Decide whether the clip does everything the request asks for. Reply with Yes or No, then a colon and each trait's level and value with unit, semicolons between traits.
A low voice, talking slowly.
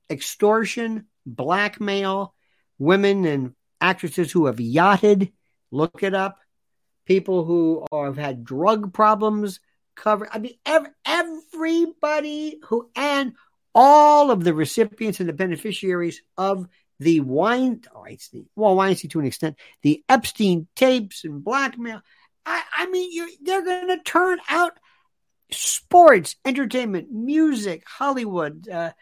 No: high, 210 Hz; slow, 125 wpm